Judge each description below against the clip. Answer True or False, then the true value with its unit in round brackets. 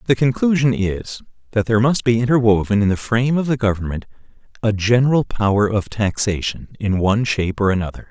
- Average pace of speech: True (180 wpm)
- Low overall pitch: True (110 Hz)